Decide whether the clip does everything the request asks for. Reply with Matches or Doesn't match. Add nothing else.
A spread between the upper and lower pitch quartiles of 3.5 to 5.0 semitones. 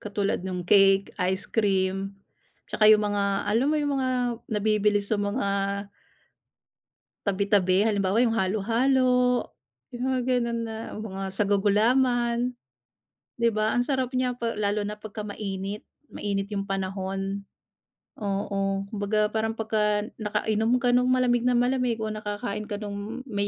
Doesn't match